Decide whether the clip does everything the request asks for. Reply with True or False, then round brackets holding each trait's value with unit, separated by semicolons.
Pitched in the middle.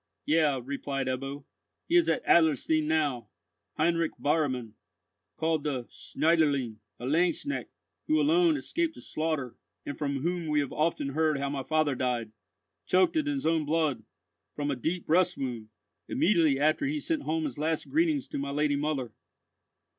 True (155 Hz)